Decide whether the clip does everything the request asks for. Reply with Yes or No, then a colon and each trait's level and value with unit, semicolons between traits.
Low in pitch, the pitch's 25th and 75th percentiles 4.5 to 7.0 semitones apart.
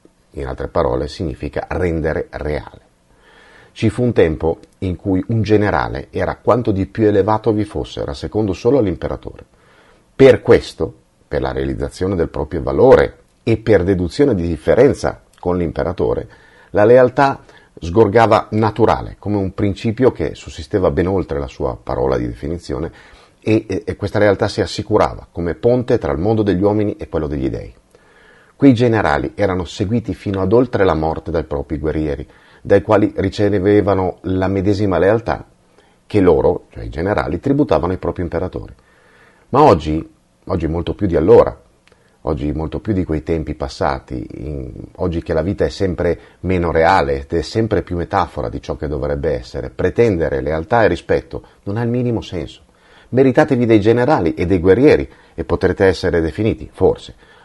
Yes: very low, 95 Hz; average, 5.2 semitones